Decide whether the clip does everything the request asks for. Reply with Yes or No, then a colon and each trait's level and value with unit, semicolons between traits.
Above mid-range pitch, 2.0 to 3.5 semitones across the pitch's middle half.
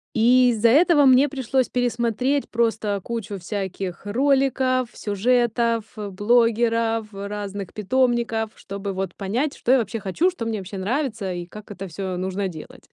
No: high, 225 Hz; average, 4.0 semitones